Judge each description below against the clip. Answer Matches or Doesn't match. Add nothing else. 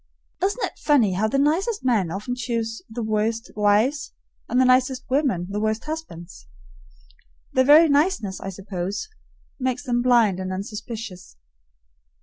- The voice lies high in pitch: Matches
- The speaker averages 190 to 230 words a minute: Doesn't match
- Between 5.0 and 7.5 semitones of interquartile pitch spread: Doesn't match